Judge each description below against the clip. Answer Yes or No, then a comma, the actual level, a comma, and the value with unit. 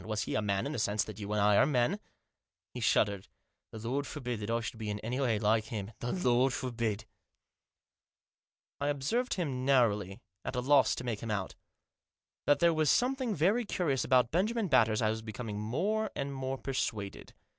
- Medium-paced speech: No, fast, 210 wpm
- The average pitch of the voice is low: Yes, low, 125 Hz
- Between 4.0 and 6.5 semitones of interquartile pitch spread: Yes, average, 5.0 semitones